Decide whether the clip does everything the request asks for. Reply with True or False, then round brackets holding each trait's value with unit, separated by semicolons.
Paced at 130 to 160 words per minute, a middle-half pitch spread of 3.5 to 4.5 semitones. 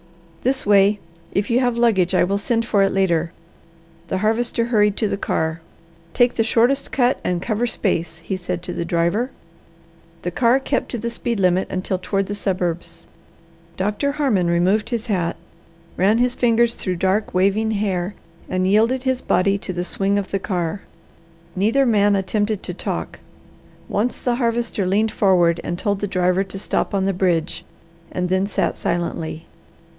False (170 wpm; 4.0 semitones)